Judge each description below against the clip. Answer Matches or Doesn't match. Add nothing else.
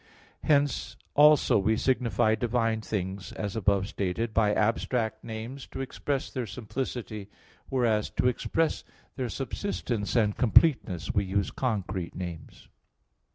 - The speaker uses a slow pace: Matches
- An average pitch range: Matches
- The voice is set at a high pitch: Doesn't match